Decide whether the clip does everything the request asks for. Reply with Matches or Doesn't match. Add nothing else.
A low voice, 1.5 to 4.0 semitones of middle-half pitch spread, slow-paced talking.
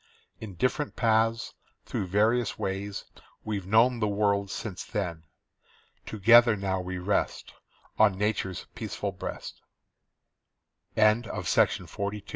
Matches